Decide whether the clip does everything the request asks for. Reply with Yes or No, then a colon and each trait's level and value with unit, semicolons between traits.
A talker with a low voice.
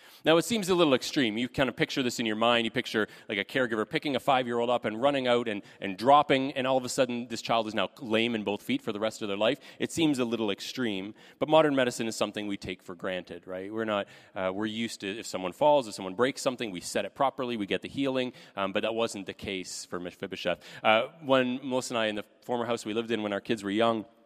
Yes: low, 115 Hz